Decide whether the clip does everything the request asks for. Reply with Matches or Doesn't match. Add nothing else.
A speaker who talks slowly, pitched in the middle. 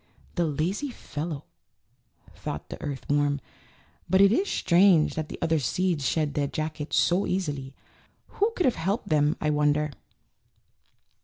Doesn't match